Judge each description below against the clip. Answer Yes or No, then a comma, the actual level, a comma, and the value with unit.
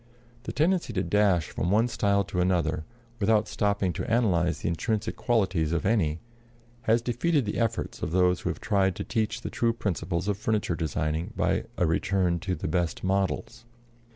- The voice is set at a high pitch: No, low, 100 Hz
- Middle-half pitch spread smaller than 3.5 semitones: No, average, 4.4 semitones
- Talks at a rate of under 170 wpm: No, average, 180 wpm